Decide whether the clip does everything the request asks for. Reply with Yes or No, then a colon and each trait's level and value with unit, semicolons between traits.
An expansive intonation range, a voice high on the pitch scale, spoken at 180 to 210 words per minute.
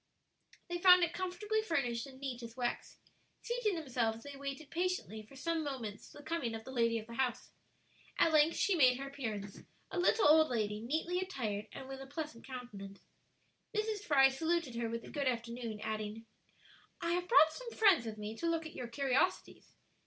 Yes: wide, 6.4 semitones; very high, 270 Hz; average, 190 wpm